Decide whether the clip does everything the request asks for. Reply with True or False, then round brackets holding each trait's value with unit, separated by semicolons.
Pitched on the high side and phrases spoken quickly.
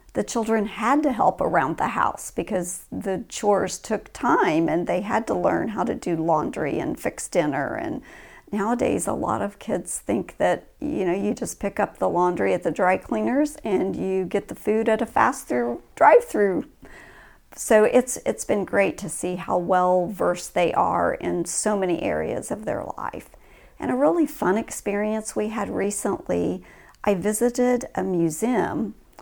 False (205 Hz; 180 wpm)